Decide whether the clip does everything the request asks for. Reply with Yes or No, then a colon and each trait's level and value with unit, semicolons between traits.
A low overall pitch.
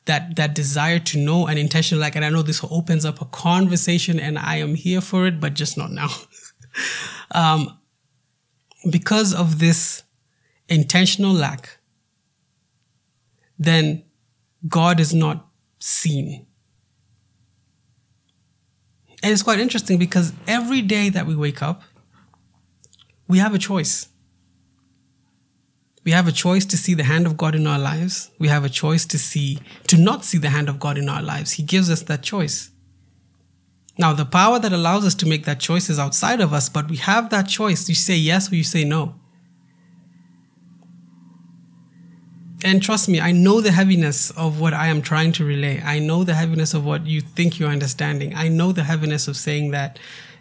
No: medium, 160 Hz